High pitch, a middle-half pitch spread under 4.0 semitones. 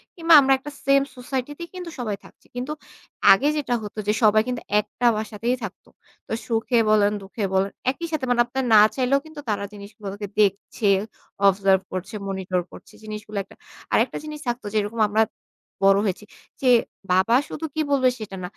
No: high, 220 Hz; average, 4.4 semitones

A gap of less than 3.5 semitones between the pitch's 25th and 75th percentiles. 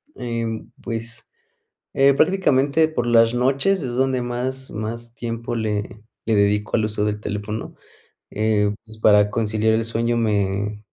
Yes: narrow, 2.5 semitones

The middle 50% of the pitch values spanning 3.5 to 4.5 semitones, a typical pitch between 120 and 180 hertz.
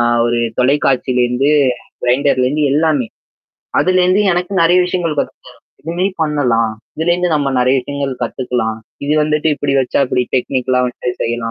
Yes: average, 4.1 semitones; medium, 140 Hz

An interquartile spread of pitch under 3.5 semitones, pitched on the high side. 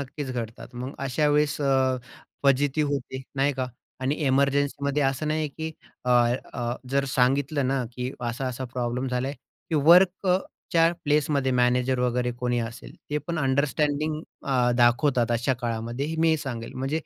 No: average, 2.8 semitones; low, 135 Hz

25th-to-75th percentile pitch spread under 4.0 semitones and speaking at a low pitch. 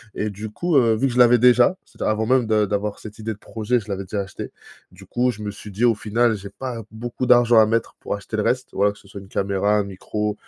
Yes: average, 2.8 semitones; low, 110 Hz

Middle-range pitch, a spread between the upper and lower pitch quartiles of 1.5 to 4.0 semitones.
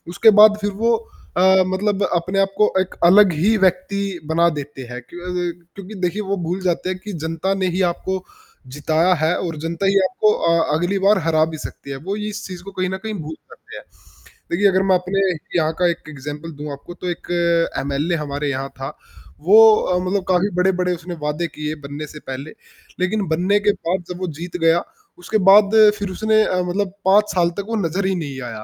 Yes: medium, 180 Hz; average, 3.5 semitones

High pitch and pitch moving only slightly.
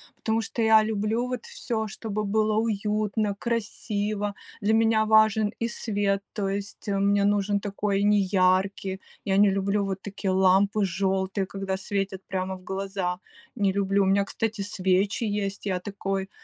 Yes: high, 200 Hz; narrow, 1.7 semitones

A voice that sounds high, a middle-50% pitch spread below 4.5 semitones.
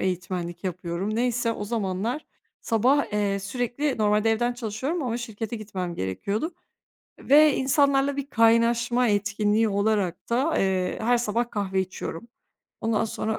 Yes: high, 220 Hz; average, 3.5 semitones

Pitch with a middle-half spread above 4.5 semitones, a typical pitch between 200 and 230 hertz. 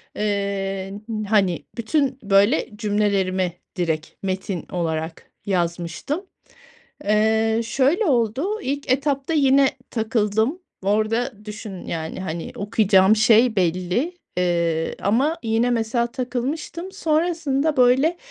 Yes: wide, 5.6 semitones; high, 220 Hz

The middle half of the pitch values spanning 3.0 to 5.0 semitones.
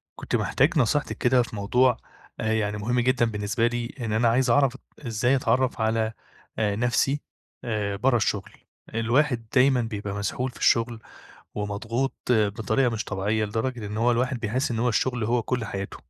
No: narrow, 2.6 semitones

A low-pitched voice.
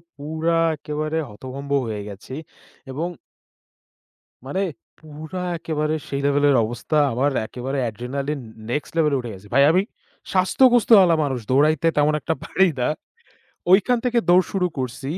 No: medium, 145 Hz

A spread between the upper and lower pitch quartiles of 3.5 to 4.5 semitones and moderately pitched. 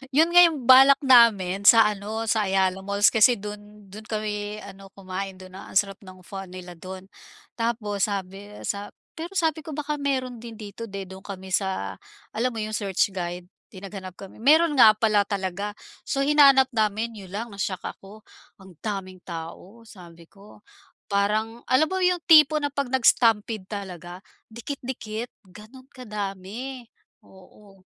No: average, 3.8 semitones; high, 210 Hz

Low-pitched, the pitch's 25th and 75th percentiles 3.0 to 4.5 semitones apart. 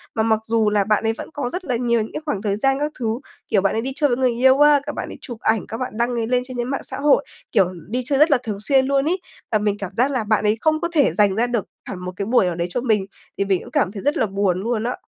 No: high, 230 Hz; average, 4.1 semitones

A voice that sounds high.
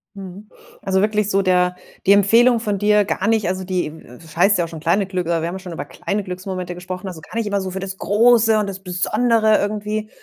Yes: high, 195 Hz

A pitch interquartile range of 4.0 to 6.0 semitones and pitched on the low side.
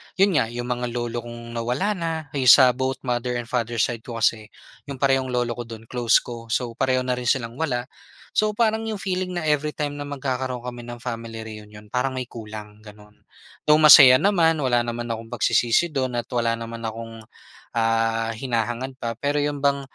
No: average, 2.9 semitones; low, 120 Hz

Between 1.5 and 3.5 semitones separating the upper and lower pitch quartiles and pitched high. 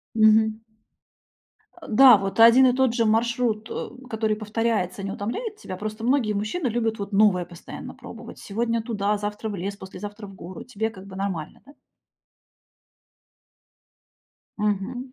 Yes: narrow, 2.5 semitones; high, 215 Hz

